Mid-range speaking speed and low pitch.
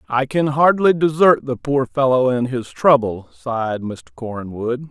Yes: average, 160 wpm; low, 130 Hz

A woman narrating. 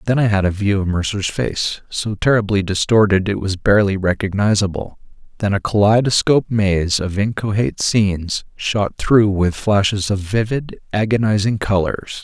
No: male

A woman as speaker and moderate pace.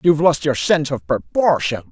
No: male; average, 190 wpm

